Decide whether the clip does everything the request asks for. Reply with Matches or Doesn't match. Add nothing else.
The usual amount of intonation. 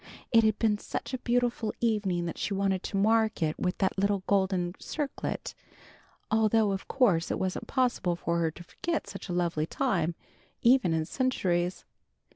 Matches